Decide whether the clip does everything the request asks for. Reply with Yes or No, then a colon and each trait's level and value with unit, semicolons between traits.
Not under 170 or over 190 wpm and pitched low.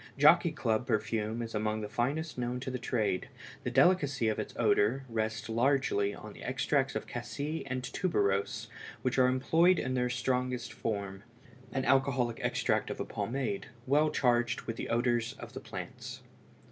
No: average, 160 wpm; low, 120 Hz